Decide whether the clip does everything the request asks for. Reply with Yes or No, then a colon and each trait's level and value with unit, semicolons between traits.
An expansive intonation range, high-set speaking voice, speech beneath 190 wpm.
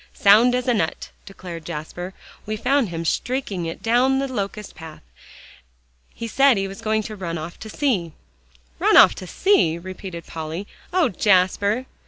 Yes: wide, 6.1 semitones; high, 200 Hz; average, 165 wpm